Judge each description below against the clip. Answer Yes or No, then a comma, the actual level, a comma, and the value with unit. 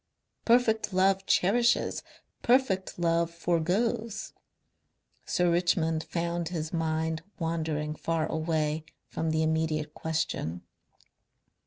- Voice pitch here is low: No, medium, 165 Hz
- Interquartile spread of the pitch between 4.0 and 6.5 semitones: No, average, 2.9 semitones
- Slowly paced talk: Yes, slow, 95 wpm